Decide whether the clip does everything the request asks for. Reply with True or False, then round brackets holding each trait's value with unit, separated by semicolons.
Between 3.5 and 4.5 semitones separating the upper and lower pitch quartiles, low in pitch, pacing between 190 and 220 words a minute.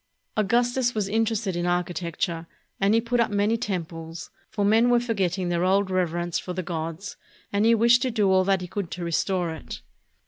False (4.2 semitones; 195 Hz; 200 wpm)